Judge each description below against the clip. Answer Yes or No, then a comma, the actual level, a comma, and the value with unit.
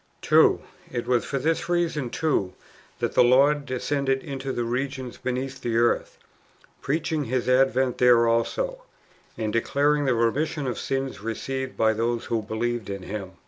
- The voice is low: Yes, low, 130 Hz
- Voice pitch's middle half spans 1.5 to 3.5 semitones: Yes, average, 3.1 semitones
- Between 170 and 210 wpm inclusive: No, average, 155 wpm